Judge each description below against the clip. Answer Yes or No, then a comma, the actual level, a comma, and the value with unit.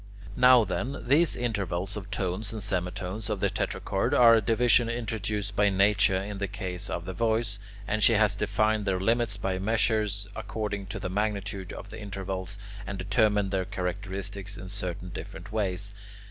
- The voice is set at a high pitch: No, low, 100 Hz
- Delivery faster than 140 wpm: Yes, average, 170 wpm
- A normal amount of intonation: No, narrow, 2.3 semitones